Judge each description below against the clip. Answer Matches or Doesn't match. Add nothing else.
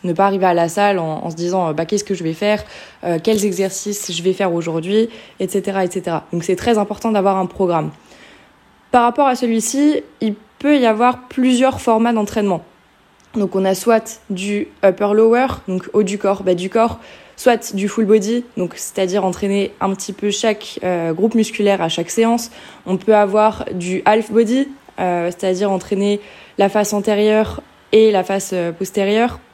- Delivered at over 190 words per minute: Doesn't match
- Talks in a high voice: Matches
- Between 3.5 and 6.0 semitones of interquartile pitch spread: Doesn't match